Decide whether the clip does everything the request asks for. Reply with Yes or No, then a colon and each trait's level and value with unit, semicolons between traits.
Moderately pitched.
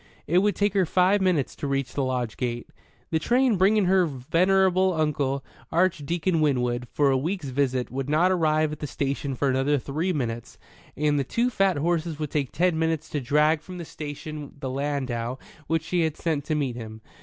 Yes: medium, 150 Hz